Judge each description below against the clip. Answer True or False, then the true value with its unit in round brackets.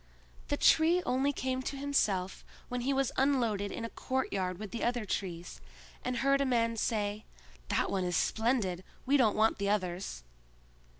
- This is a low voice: False (230 Hz)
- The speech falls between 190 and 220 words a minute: False (170 wpm)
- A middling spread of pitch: True (4.9 semitones)